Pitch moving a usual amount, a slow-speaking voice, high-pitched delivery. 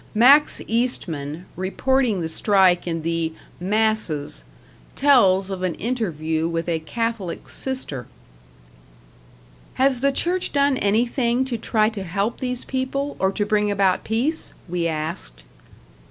No: wide, 6.9 semitones; slow, 125 wpm; high, 205 Hz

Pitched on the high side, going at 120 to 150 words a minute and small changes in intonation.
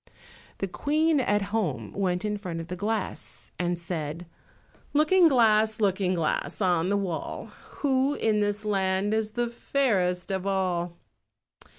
No: high, 200 Hz; average, 145 wpm; average, 3.7 semitones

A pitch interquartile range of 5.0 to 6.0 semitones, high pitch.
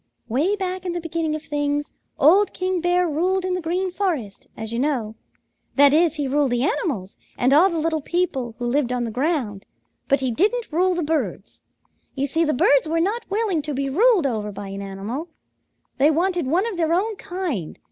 Yes: wide, 5.4 semitones; very high, 310 Hz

